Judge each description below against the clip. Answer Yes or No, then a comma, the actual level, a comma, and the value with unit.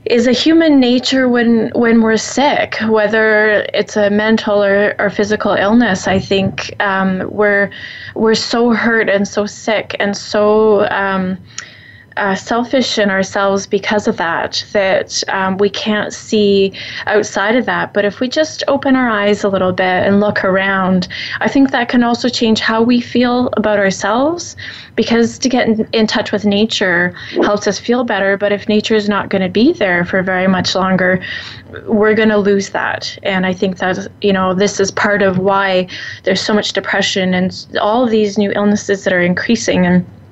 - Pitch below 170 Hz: No, high, 205 Hz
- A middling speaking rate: Yes, average, 185 wpm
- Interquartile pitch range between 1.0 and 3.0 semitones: Yes, narrow, 2.4 semitones